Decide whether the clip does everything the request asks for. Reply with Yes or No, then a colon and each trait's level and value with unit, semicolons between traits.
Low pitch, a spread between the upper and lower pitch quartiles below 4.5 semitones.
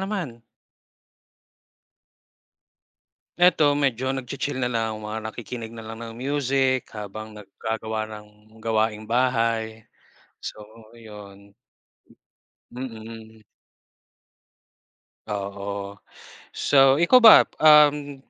Yes: low, 115 Hz; average, 3.6 semitones